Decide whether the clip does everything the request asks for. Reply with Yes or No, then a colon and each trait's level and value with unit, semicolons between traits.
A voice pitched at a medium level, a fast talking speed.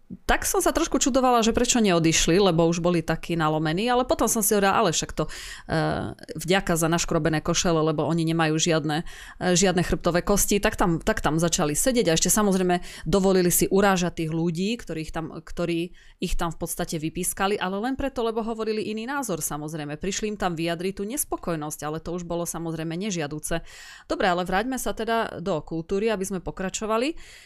Yes: medium, 180 Hz; fast, 190 wpm